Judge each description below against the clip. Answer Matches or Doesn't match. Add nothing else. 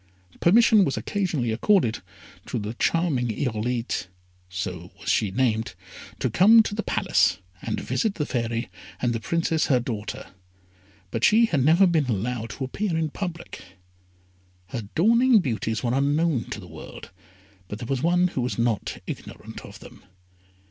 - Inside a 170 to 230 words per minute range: Doesn't match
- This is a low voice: Matches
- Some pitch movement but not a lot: Doesn't match